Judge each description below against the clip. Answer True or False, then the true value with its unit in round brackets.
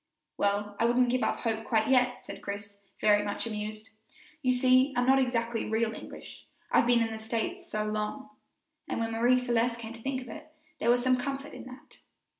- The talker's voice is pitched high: True (235 Hz)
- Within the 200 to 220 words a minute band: True (205 wpm)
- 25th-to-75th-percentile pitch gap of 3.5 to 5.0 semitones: False (2.5 semitones)